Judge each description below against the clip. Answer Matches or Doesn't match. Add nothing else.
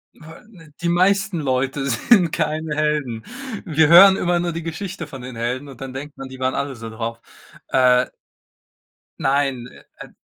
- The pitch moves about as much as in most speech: Matches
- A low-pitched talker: Doesn't match